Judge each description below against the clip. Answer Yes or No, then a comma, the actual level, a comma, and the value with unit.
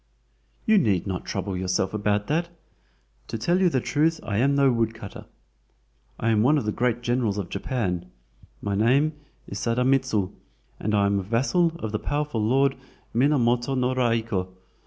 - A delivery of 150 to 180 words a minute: Yes, average, 165 wpm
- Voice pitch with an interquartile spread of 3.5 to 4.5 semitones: No, average, 4.9 semitones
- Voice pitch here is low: Yes, low, 115 Hz